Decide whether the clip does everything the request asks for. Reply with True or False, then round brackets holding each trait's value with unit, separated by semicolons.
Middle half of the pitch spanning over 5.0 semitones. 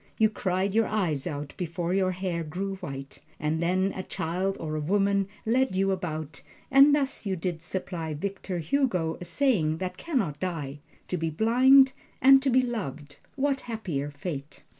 True (5.4 semitones)